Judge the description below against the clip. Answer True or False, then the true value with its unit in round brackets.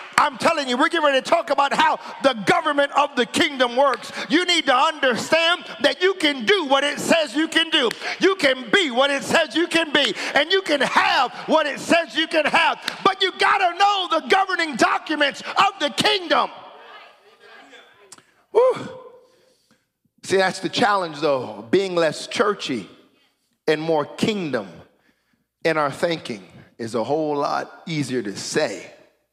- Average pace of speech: True (165 wpm)